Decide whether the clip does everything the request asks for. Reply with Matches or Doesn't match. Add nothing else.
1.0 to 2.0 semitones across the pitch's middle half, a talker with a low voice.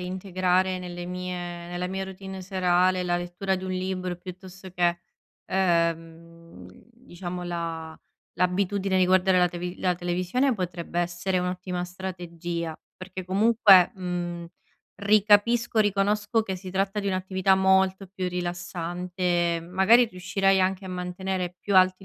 Doesn't match